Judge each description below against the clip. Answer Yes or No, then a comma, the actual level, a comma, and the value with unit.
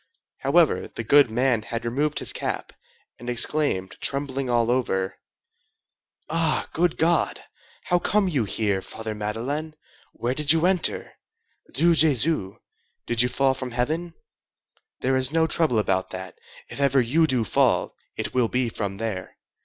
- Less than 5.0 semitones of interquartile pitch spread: No, average, 5.3 semitones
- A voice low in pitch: Yes, low, 130 Hz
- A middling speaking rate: Yes, average, 145 wpm